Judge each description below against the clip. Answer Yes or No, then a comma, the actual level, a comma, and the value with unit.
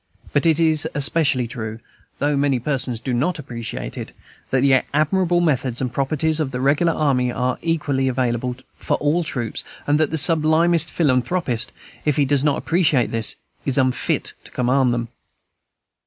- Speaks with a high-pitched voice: No, medium, 140 Hz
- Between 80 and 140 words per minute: No, average, 165 wpm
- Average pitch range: Yes, average, 3.7 semitones